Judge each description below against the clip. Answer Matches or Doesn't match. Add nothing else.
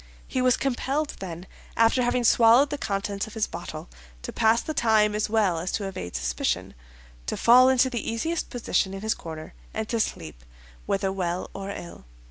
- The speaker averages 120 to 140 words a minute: Doesn't match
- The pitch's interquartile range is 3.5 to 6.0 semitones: Matches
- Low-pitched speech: Doesn't match